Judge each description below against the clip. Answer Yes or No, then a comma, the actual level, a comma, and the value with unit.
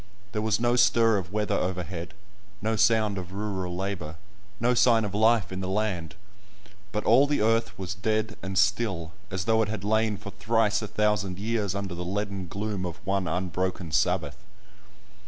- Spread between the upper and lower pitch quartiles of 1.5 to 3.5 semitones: Yes, average, 3.0 semitones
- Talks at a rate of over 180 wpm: No, average, 175 wpm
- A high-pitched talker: No, low, 100 Hz